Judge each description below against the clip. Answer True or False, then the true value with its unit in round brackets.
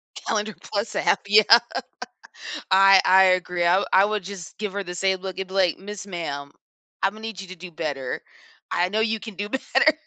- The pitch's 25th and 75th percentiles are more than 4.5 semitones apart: False (2.6 semitones)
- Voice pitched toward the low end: False (195 Hz)